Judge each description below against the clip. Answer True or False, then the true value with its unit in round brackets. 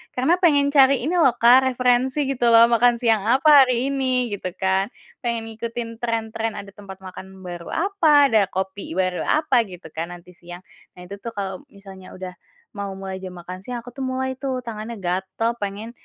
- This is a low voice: False (225 Hz)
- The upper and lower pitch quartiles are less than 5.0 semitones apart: False (5.3 semitones)